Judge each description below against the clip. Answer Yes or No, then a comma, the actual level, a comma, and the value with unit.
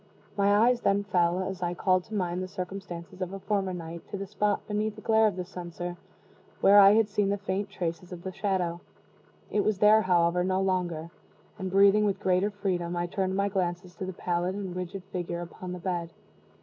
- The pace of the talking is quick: Yes, fast, 210 wpm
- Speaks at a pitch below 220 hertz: Yes, medium, 185 Hz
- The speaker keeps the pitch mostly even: Yes, narrow, 2.2 semitones